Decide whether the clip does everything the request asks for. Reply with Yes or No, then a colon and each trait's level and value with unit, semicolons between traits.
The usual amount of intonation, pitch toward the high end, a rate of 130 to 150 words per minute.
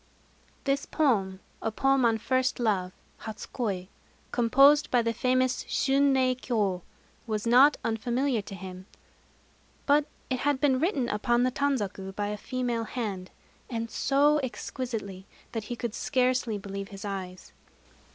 Yes: average, 4.2 semitones; high, 240 Hz; average, 140 wpm